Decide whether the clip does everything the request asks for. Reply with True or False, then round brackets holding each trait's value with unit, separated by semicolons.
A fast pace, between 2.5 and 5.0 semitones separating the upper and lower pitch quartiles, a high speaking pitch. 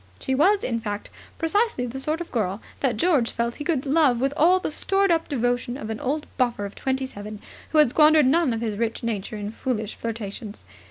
False (215 wpm; 5.4 semitones; 255 Hz)